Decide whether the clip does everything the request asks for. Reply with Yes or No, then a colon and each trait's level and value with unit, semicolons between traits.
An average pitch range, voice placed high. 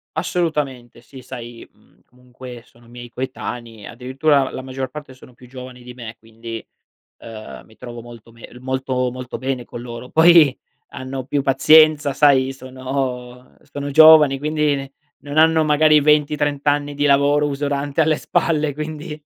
No: average, 3.0 semitones; low, 135 Hz